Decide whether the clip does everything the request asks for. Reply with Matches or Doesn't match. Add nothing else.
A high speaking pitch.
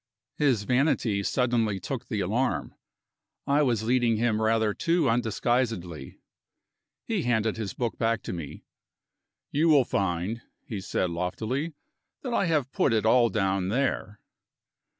Doesn't match